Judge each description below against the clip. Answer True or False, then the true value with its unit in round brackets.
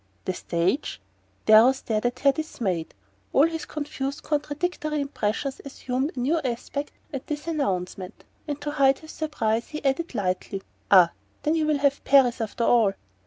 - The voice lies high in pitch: True (270 Hz)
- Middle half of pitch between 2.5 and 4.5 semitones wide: False (5.3 semitones)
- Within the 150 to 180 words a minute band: True (160 wpm)